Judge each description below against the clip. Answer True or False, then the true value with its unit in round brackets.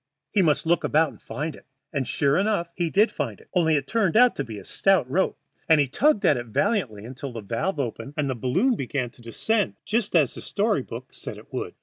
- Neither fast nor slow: False (240 wpm)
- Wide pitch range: True (7.3 semitones)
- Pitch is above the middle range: False (150 Hz)